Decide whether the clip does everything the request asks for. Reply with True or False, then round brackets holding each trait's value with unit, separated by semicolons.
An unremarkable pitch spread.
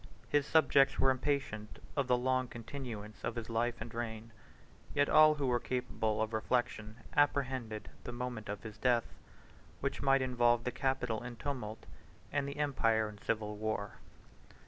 True (3.4 semitones)